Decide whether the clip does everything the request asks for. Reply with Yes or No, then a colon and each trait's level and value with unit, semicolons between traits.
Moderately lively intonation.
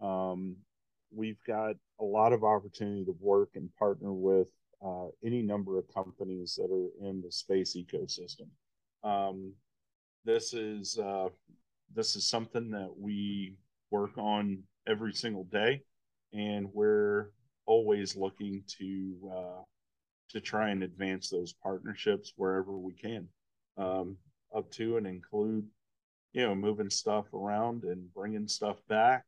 No: narrow, 2.1 semitones